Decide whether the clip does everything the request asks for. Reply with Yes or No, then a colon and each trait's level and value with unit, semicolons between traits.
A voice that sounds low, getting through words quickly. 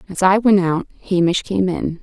No: medium, 185 Hz; fast, 210 wpm